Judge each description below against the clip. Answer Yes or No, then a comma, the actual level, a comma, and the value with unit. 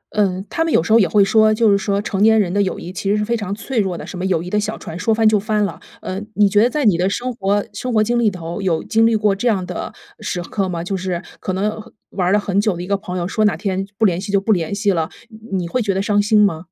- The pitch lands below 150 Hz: No, high, 200 Hz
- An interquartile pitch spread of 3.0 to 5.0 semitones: No, narrow, 2.6 semitones